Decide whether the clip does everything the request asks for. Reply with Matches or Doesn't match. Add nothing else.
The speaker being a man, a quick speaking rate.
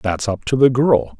Matches